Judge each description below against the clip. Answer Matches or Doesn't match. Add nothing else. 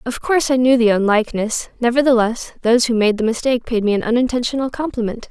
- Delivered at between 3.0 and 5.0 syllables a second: Doesn't match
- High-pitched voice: Matches